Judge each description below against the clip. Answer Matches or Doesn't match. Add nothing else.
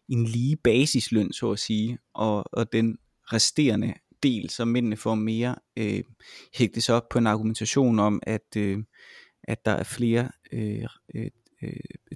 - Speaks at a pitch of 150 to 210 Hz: Doesn't match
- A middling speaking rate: Matches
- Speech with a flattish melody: Matches